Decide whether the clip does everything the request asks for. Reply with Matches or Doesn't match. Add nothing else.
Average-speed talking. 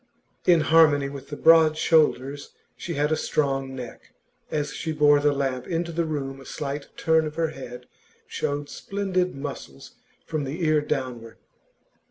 Matches